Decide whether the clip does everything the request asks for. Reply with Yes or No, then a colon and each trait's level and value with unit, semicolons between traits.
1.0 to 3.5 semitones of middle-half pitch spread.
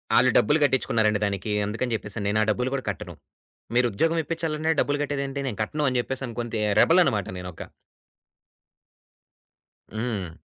No: average, 5.3 semitones